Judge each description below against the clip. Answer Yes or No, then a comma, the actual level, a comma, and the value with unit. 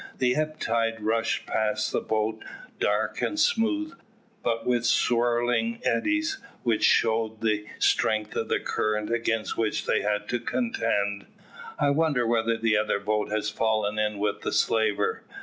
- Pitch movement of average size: No, narrow, 2.2 semitones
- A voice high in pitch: No, low, 115 Hz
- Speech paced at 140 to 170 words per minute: Yes, average, 150 wpm